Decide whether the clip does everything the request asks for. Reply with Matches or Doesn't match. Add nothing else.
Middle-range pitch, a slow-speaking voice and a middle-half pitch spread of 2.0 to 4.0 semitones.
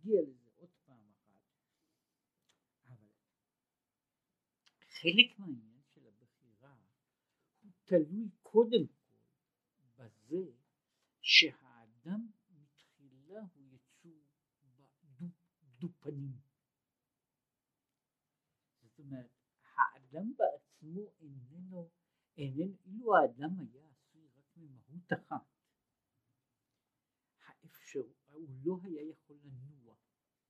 Doesn't match